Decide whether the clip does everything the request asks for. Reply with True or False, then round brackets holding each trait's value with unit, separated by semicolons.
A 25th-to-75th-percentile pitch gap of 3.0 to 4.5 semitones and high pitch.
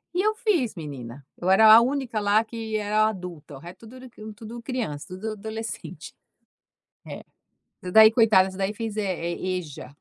True (3.7 semitones; 215 Hz)